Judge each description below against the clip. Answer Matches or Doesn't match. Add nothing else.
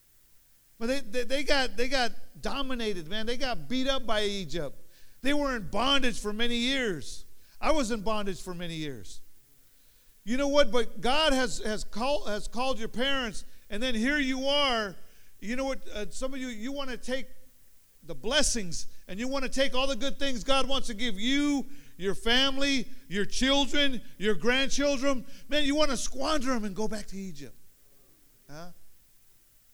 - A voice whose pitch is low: Doesn't match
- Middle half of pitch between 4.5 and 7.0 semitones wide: Matches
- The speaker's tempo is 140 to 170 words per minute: Doesn't match